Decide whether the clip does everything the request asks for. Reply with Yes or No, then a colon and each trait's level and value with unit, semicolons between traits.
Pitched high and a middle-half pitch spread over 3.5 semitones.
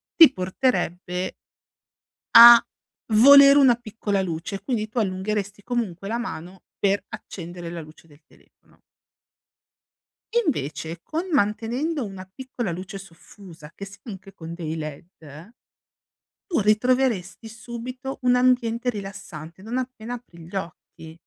Yes: high, 205 Hz; wide, 5.5 semitones